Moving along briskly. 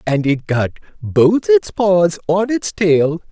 No: average, 165 wpm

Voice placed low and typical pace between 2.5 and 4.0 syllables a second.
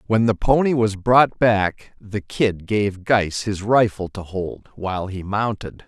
Yes: low, 105 Hz; 3.7 syllables/s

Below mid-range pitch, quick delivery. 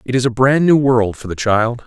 Yes: low, 120 Hz; fast, 290 wpm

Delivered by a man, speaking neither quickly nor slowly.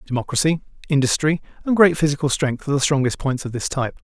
Yes: male; average, 190 wpm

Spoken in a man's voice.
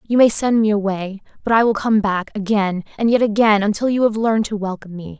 No: female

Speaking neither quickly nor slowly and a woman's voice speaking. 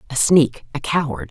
Yes: average, 185 wpm; female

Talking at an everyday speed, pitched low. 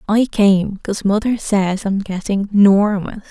No: average, 145 wpm; high, 200 Hz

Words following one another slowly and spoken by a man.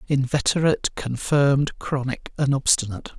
Yes: slow, 95 wpm; male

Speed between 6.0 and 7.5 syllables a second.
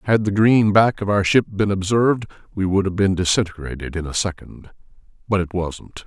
No: 5.3 syllables/s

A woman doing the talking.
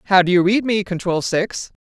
Yes: female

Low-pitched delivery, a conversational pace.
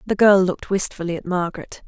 No: medium, 185 Hz; average, 190 wpm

